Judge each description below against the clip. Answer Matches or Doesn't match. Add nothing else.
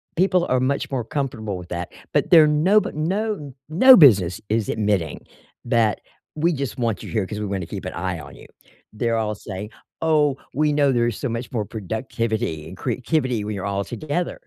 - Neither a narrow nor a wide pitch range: Doesn't match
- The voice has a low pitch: Matches